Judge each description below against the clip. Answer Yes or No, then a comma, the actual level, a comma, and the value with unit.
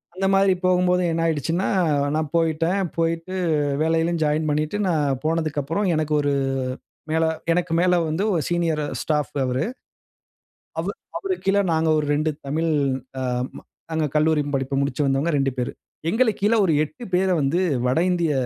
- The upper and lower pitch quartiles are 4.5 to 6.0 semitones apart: No, average, 3.0 semitones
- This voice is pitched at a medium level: Yes, medium, 160 Hz